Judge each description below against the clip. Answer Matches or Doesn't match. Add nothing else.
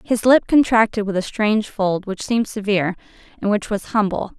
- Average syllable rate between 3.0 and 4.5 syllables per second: Doesn't match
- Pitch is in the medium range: Doesn't match